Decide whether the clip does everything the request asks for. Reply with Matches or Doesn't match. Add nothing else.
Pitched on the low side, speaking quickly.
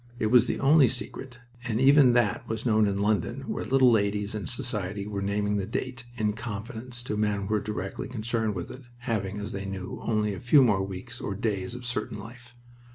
Matches